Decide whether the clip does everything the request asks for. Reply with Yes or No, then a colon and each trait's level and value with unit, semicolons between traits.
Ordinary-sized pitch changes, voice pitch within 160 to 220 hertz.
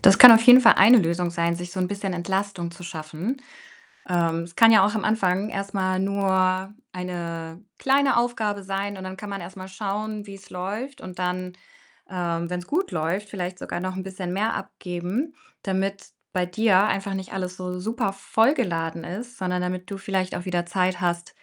No: narrow, 2.2 semitones; high, 190 Hz